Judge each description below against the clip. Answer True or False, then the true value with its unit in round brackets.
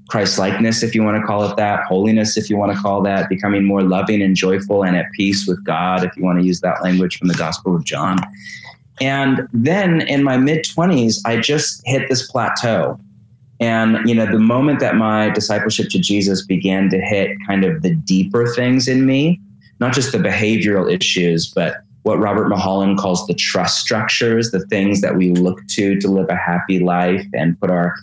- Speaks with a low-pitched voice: True (100 Hz)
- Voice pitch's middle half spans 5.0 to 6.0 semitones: False (3.7 semitones)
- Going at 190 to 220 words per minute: True (205 wpm)